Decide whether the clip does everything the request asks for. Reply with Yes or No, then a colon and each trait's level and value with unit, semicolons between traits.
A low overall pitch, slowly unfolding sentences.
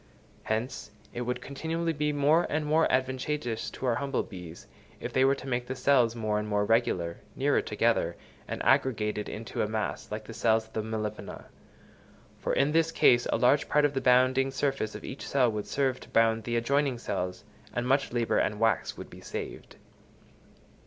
No: low, 125 Hz; average, 190 wpm